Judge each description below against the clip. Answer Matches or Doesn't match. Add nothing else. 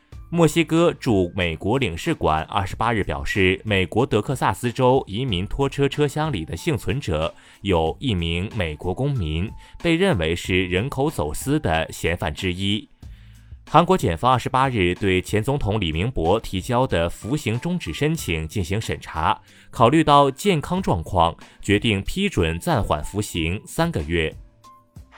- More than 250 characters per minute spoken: Doesn't match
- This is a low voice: Matches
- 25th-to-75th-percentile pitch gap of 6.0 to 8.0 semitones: Matches